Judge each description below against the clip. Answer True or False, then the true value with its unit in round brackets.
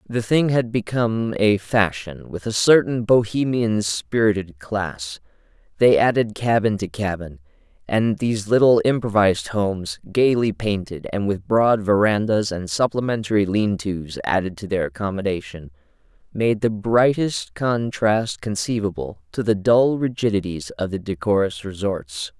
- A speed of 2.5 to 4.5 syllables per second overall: True (4.4 syllables/s)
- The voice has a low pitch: True (105 Hz)